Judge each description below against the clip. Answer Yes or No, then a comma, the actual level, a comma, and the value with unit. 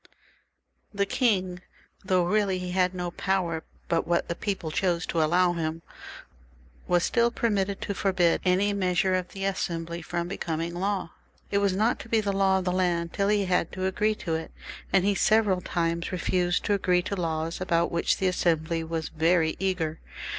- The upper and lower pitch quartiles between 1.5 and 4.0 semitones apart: Yes, narrow, 2.5 semitones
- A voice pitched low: No, medium, 180 Hz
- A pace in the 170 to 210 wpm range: Yes, average, 180 wpm